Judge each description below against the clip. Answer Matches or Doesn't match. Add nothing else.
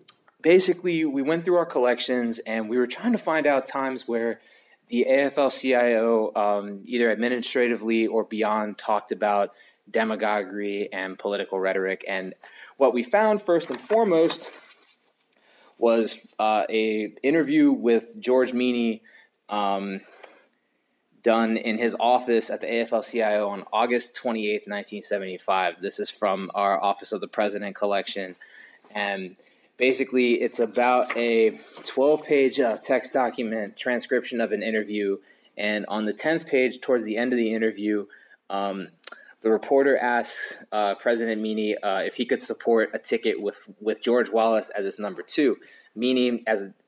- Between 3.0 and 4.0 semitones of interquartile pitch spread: Matches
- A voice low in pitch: Matches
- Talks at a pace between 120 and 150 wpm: Matches